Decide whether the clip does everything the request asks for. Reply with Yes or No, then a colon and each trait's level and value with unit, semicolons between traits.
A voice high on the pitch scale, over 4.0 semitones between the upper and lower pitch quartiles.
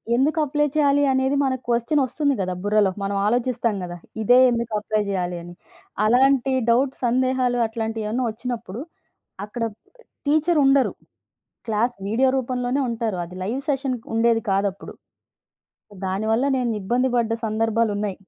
No: high, 235 Hz; average, 3.5 semitones